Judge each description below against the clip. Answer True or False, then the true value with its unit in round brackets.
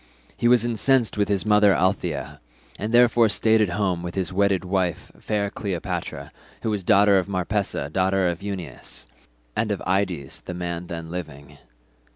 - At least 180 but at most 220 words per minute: False (165 wpm)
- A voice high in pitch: False (95 Hz)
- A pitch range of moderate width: True (3.0 semitones)